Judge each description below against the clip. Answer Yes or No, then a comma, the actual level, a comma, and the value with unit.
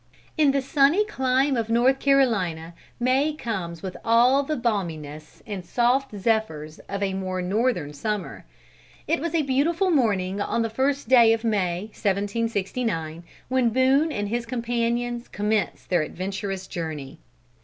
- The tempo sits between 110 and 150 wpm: Yes, average, 145 wpm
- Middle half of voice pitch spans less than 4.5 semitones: No, wide, 5.5 semitones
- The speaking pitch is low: No, high, 230 Hz